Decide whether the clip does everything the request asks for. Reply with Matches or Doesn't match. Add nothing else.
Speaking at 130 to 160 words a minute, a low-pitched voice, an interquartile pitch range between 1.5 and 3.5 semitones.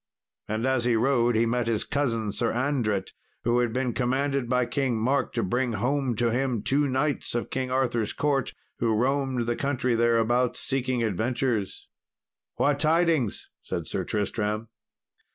Matches